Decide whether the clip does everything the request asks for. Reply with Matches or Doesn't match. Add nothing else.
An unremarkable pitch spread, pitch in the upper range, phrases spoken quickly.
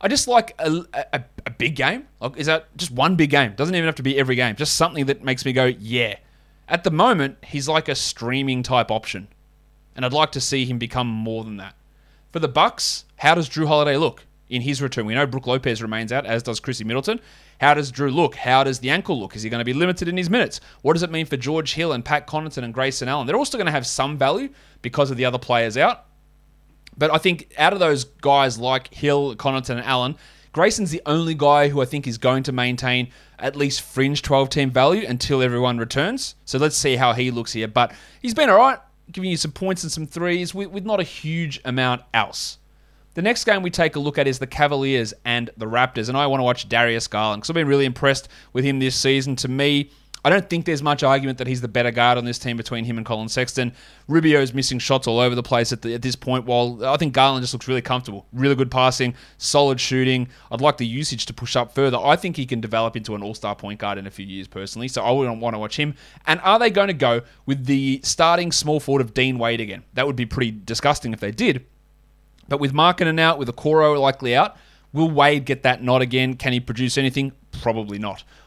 Doesn't match